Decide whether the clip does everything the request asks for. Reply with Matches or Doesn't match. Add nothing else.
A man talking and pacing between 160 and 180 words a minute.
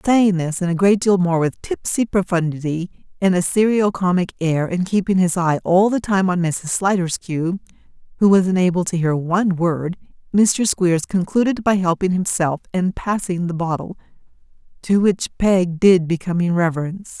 Doesn't match